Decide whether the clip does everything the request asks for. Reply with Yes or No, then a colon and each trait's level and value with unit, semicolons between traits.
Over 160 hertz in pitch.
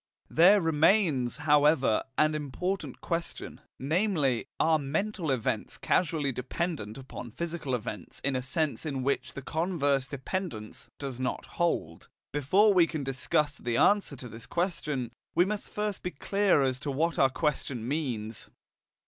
No: medium, 145 Hz